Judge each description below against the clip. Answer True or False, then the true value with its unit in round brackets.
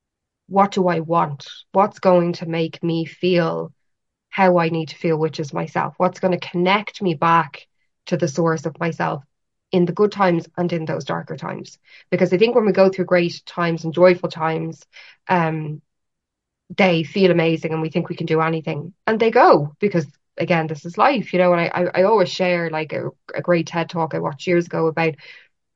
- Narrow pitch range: True (2.1 semitones)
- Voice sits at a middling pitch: True (175 Hz)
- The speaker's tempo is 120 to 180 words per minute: False (205 wpm)